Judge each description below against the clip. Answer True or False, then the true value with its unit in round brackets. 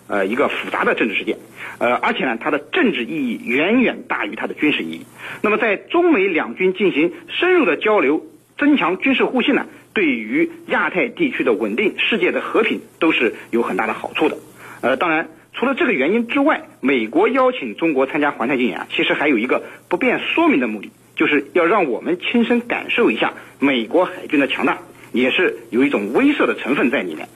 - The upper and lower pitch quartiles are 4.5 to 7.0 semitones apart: True (5.6 semitones)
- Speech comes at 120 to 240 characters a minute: False (315 characters per minute)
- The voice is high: True (290 Hz)